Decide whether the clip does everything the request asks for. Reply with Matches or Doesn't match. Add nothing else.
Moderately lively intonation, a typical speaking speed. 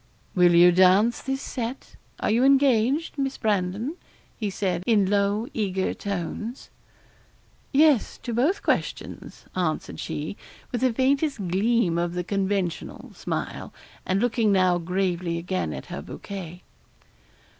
Doesn't match